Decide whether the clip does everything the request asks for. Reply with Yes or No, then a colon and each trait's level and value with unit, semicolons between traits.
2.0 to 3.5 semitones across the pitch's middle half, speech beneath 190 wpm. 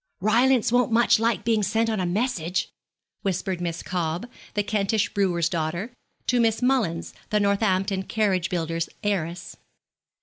No: average, 4.4 semitones; average, 140 wpm